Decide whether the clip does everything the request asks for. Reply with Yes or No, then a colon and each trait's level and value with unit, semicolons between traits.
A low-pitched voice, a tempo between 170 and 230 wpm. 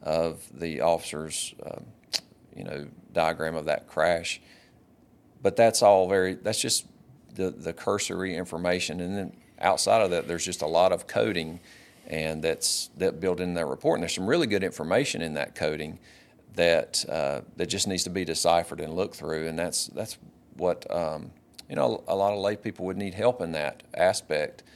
Yes: very low, 85 Hz; average, 185 wpm